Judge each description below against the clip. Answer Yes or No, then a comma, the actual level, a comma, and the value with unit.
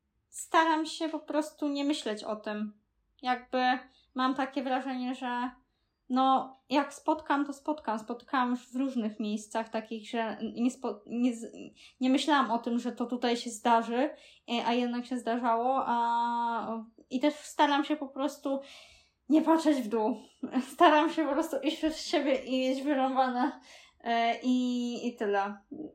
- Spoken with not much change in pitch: No, average, 3.3 semitones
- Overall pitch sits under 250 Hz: No, very high, 255 Hz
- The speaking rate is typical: Yes, average, 150 wpm